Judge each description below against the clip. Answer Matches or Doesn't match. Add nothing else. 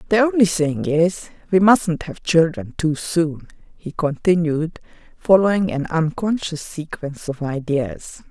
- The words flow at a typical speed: Doesn't match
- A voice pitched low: Doesn't match